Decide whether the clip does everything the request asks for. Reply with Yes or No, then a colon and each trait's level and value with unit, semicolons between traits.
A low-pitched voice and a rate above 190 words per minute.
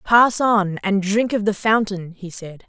No: high, 200 Hz; average, 200 wpm